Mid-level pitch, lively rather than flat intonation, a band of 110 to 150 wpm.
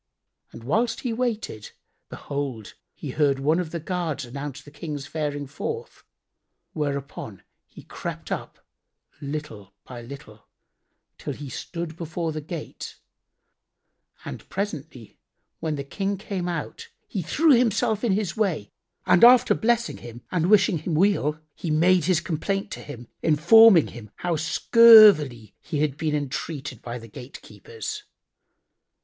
Yes: medium, 160 Hz; wide, 5.9 semitones; average, 140 wpm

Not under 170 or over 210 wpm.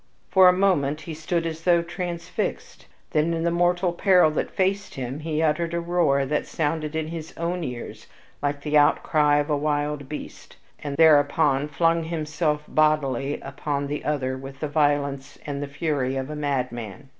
Yes: average, 175 wpm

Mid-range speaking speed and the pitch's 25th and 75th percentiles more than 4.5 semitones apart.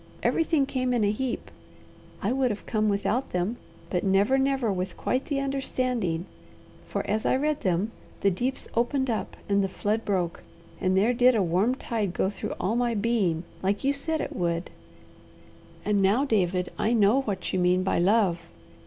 Yes: average, 180 wpm; average, 5.2 semitones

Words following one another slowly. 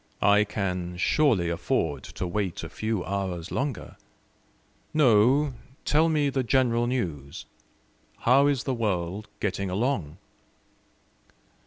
Yes: slow, 115 wpm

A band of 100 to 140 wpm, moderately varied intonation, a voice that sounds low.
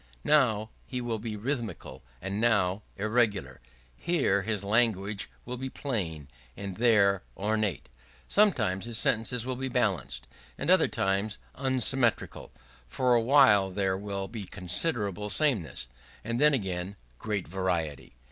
Yes: slow, 135 wpm; average, 4.0 semitones; low, 105 Hz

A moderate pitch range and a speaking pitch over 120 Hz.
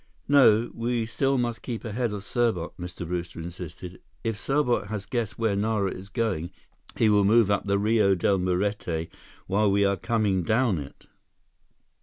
No: average, 3.7 semitones; low, 105 Hz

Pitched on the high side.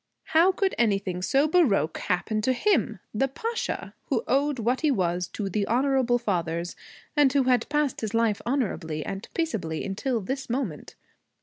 Yes: high, 240 Hz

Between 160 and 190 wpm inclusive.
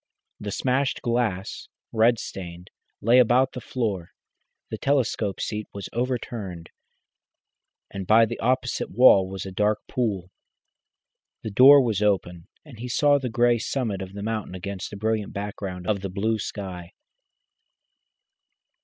No: slow, 135 wpm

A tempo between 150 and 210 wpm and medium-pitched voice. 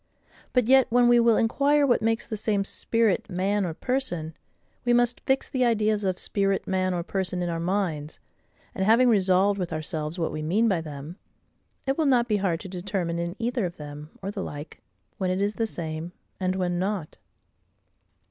No: average, 195 wpm; high, 195 Hz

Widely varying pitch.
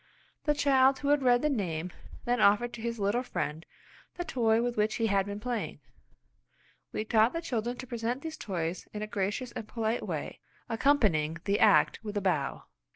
No: average, 3.6 semitones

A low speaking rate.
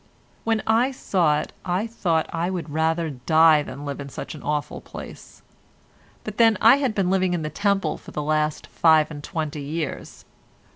No: average, 180 wpm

